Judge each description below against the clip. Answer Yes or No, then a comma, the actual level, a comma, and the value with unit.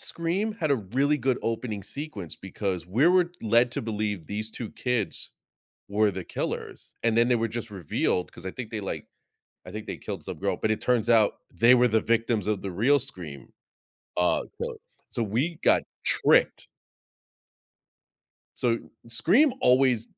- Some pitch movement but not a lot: Yes, average, 3.7 semitones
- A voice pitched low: Yes, low, 115 Hz